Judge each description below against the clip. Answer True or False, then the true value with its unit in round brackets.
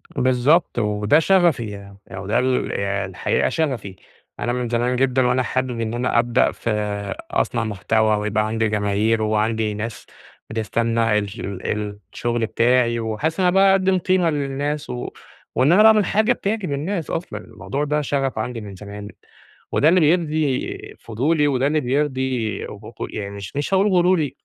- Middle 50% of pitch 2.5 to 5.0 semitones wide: False (5.6 semitones)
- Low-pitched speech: True (125 Hz)